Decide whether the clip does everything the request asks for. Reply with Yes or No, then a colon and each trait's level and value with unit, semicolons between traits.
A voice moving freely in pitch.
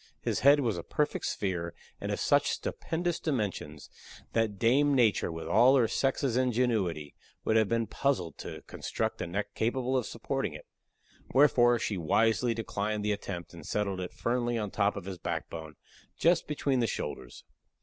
No: average, 4.7 semitones